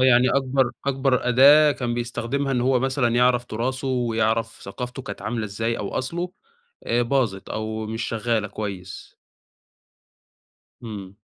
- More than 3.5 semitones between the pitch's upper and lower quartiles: No, average, 2.8 semitones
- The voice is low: Yes, low, 120 Hz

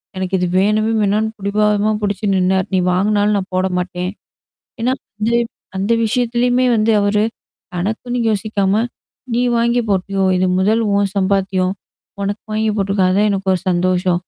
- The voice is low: No, high, 200 Hz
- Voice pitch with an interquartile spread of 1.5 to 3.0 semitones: Yes, narrow, 2.4 semitones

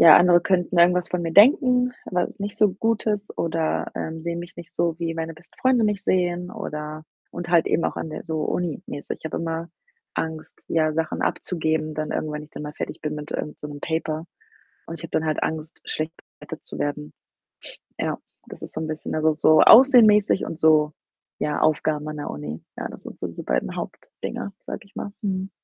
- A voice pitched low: No, medium, 165 Hz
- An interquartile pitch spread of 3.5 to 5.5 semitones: No, narrow, 2.6 semitones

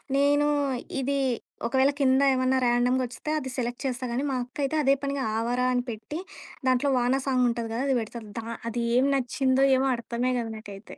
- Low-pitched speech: No, very high, 255 Hz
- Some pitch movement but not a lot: No, narrow, 2.0 semitones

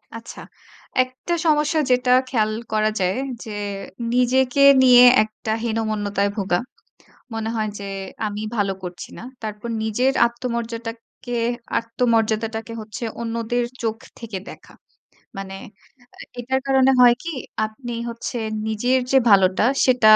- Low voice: No, high, 230 Hz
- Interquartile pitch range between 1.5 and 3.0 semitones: Yes, narrow, 2.5 semitones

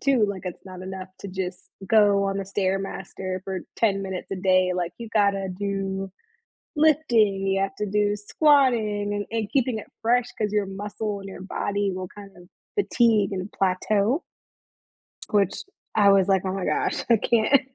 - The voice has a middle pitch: No, high, 200 Hz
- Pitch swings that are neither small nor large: No, narrow, 2.0 semitones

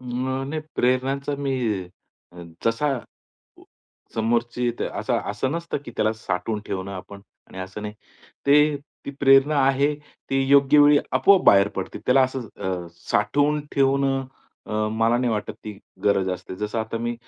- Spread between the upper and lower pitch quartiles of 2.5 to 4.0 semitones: No, average, 4.6 semitones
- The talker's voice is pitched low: Yes, low, 125 Hz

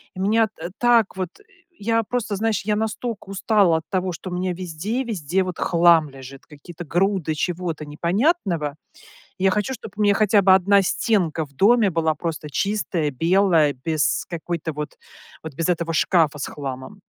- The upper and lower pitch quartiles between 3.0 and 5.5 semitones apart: Yes, average, 4.4 semitones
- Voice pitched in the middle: Yes, medium, 180 Hz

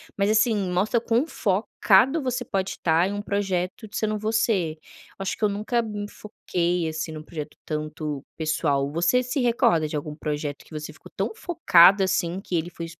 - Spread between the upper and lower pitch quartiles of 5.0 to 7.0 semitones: Yes, wide, 5.4 semitones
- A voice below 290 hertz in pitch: Yes, high, 190 Hz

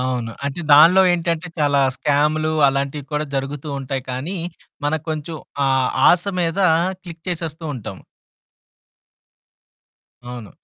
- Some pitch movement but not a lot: Yes, average, 3.4 semitones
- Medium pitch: Yes, medium, 150 Hz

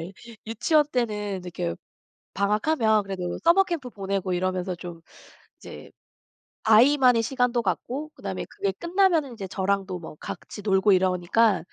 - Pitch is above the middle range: Yes, high, 210 Hz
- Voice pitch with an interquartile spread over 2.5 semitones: Yes, wide, 5.5 semitones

